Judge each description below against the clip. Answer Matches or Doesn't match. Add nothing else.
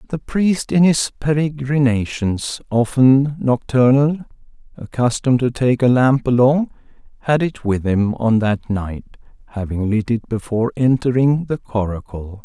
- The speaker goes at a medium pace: Doesn't match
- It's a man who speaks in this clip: Matches